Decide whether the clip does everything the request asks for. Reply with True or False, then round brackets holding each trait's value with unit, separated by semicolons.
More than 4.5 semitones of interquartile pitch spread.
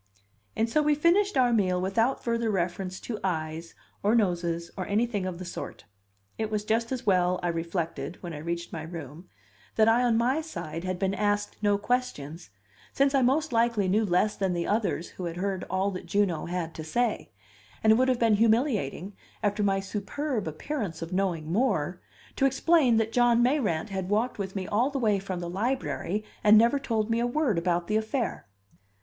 True (4.9 semitones)